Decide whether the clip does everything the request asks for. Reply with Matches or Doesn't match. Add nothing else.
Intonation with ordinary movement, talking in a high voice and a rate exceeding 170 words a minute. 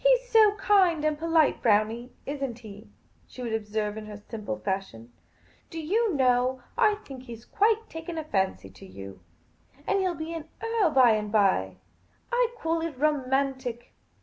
Doesn't match